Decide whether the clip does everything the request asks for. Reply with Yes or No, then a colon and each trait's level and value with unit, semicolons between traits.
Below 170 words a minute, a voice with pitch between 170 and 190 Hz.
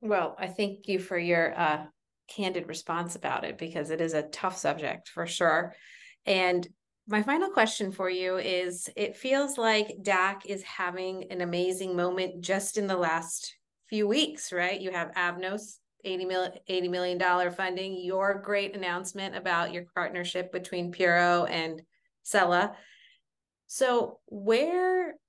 Yes: average, 145 wpm; medium, 185 Hz